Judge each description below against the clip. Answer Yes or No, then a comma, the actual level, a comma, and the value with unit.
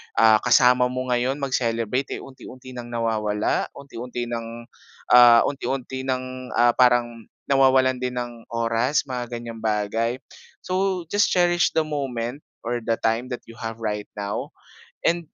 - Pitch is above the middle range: No, low, 120 Hz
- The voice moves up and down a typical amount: No, narrow, 2.2 semitones